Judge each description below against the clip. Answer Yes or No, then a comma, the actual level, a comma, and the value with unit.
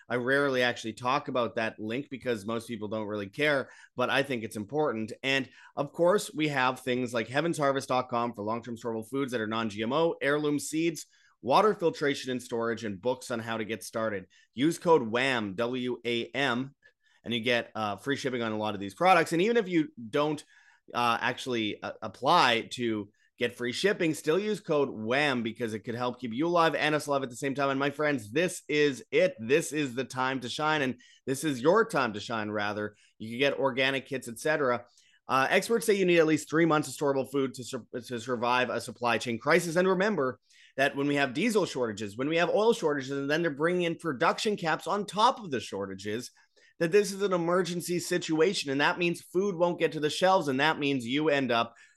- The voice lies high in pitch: No, low, 135 Hz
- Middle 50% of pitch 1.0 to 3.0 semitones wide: No, average, 4.9 semitones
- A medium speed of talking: No, fast, 220 wpm